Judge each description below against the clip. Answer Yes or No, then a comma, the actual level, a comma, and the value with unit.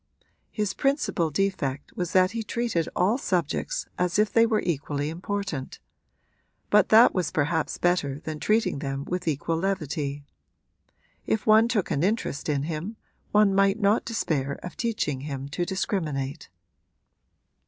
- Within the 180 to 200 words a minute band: No, average, 145 wpm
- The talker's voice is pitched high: No, medium, 180 Hz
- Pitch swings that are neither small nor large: No, wide, 6.0 semitones